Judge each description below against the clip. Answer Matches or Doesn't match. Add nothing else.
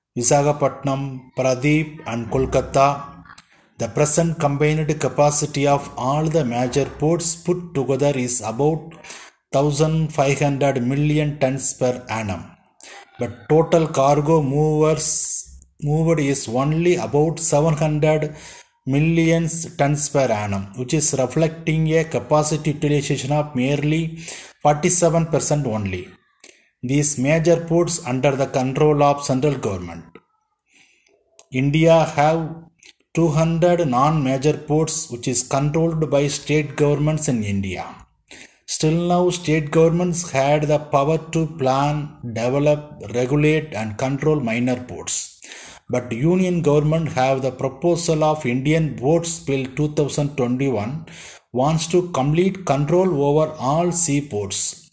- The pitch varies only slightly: Doesn't match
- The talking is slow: Matches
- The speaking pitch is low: Doesn't match